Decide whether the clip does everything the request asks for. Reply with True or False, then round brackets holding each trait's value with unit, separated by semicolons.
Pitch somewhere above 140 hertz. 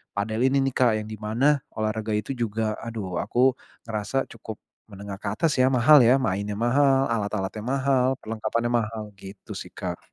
False (115 Hz)